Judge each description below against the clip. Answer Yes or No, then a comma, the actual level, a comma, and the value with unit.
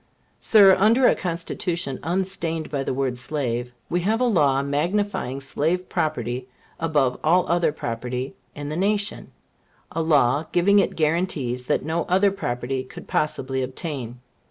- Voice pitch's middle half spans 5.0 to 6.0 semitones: Yes, wide, 5.5 semitones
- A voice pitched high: No, medium, 155 Hz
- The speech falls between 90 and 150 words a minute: Yes, average, 145 wpm